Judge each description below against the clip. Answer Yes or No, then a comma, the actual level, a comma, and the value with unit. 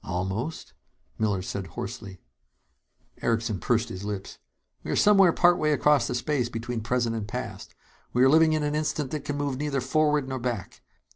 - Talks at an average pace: Yes, average, 170 wpm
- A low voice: Yes, low, 125 Hz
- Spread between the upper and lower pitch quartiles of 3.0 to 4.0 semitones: No, average, 5.3 semitones